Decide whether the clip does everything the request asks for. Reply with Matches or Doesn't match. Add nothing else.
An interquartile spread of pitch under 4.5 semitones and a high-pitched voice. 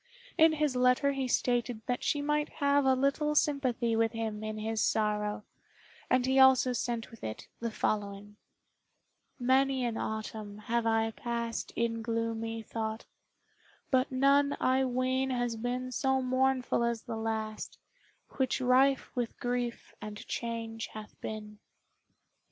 Matches